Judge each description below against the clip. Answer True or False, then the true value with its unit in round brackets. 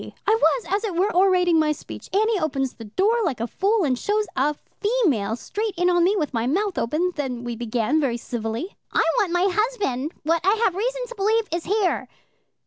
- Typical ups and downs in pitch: False (7.6 semitones)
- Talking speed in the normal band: False (210 wpm)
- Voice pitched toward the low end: False (355 Hz)